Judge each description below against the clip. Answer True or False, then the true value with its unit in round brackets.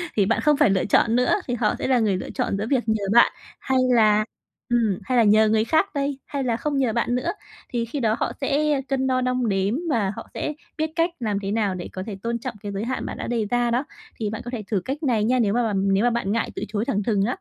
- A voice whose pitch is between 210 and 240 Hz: True (235 Hz)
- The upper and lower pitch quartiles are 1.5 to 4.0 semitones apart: True (3.5 semitones)